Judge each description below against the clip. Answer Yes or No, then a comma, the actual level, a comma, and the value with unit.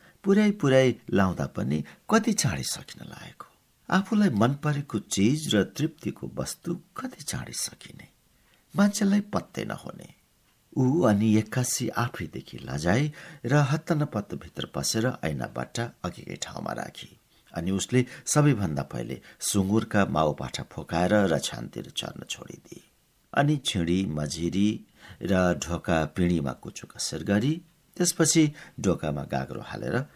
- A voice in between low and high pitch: No, low, 120 Hz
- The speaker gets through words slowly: Yes, slow, 110 wpm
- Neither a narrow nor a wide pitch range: No, wide, 8.7 semitones